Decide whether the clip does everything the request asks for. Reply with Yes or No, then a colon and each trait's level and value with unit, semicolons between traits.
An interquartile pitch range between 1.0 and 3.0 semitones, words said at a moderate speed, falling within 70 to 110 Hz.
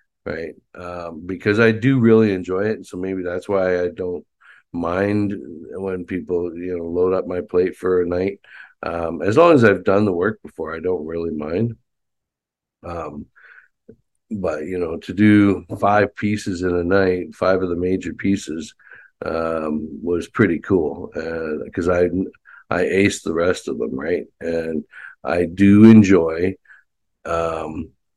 Yes: narrow, 2.5 semitones; average, 160 wpm; very low, 90 Hz